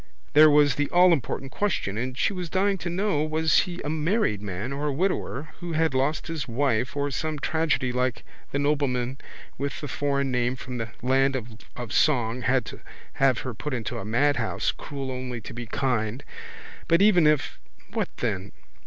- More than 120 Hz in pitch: Yes, medium, 140 Hz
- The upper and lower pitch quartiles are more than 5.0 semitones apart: No, average, 3.8 semitones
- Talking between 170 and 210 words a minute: Yes, average, 180 wpm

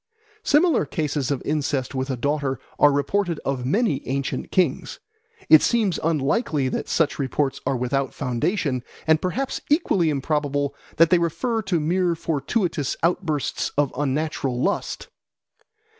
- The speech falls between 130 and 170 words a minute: Yes, slow, 135 wpm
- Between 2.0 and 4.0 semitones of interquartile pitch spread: No, average, 4.5 semitones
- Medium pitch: Yes, medium, 150 Hz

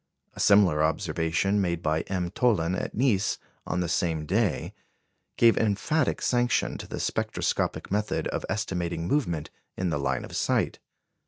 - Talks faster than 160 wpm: No, average, 150 wpm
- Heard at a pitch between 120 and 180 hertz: No, very low, 90 Hz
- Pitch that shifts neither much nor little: Yes, average, 4.3 semitones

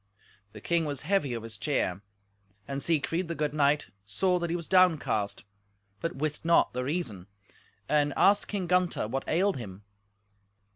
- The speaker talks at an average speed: Yes, average, 160 wpm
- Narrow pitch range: No, wide, 5.4 semitones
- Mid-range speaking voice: Yes, medium, 150 Hz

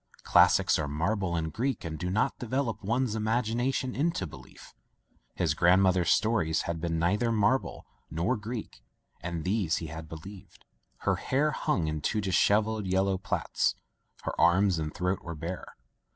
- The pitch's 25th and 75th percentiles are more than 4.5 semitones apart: Yes, average, 4.9 semitones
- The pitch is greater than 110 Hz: No, very low, 95 Hz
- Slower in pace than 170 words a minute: Yes, average, 155 wpm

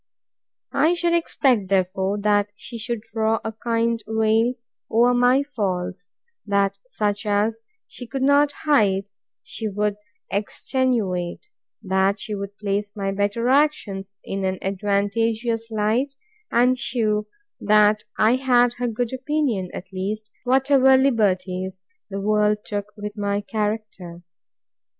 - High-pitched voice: Yes, high, 215 Hz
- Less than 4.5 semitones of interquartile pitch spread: Yes, average, 3.5 semitones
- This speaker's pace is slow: Yes, slow, 125 wpm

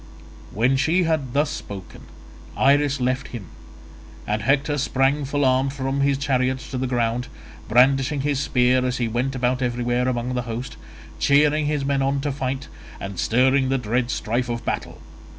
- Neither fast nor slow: Yes, average, 170 wpm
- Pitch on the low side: Yes, low, 130 Hz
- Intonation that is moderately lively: No, narrow, 2.2 semitones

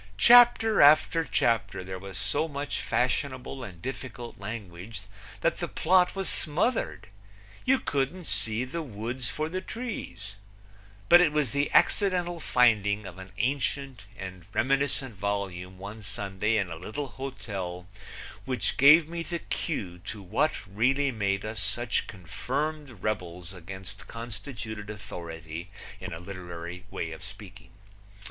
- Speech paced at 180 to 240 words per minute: No, slow, 135 wpm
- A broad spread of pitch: Yes, wide, 6.9 semitones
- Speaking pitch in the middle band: No, low, 110 Hz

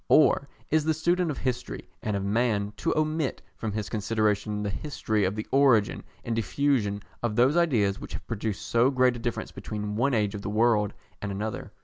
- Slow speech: No, average, 200 wpm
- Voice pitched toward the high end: No, low, 115 Hz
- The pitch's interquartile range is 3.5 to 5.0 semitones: Yes, average, 4.5 semitones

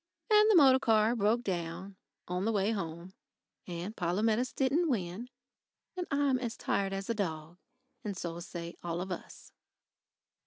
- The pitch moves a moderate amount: No, wide, 5.8 semitones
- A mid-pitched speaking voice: No, high, 200 Hz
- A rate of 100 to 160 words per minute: Yes, average, 155 wpm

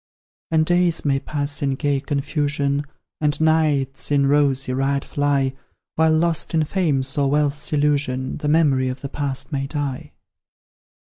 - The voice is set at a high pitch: No, medium, 145 Hz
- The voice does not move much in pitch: Yes, narrow, 1.7 semitones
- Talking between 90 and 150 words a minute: Yes, average, 145 wpm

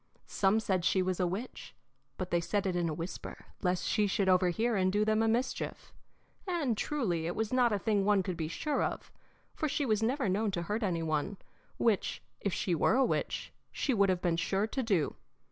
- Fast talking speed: Yes, fast, 215 wpm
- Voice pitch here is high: Yes, high, 200 Hz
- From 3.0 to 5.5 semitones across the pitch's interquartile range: Yes, average, 3.8 semitones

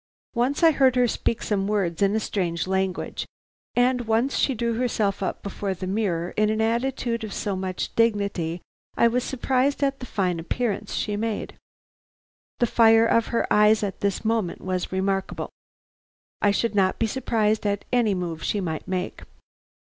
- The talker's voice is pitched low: No, high, 215 Hz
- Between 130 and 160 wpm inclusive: No, average, 170 wpm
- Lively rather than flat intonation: No, average, 3.6 semitones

